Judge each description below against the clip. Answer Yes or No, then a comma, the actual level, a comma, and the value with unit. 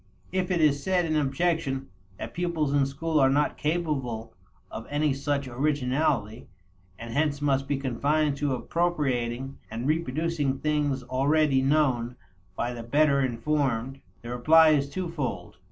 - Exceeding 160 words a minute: No, average, 140 wpm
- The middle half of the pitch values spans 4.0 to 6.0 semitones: No, average, 2.9 semitones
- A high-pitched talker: No, medium, 140 Hz